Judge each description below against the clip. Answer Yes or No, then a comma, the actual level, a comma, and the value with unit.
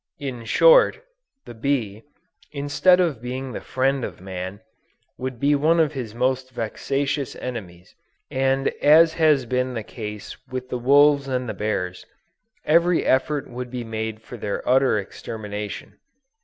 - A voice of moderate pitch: No, low, 130 Hz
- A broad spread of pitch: No, average, 4.2 semitones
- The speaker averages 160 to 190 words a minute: No, average, 145 wpm